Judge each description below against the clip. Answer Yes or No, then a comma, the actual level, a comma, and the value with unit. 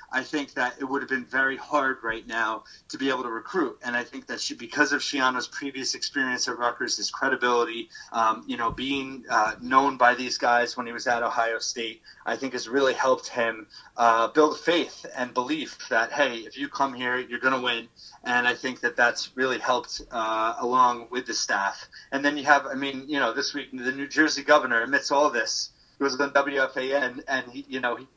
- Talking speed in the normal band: No, fast, 220 wpm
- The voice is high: No, low, 130 Hz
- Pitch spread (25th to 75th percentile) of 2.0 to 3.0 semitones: Yes, narrow, 2.6 semitones